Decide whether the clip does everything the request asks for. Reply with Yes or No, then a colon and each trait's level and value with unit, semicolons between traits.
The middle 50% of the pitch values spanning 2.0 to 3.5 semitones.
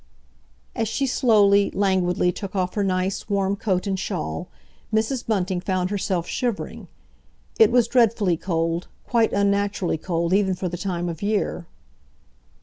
Yes: average, 2.7 semitones